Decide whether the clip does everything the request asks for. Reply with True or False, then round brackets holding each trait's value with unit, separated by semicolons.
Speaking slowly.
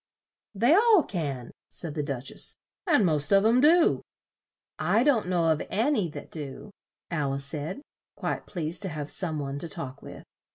False (180 wpm)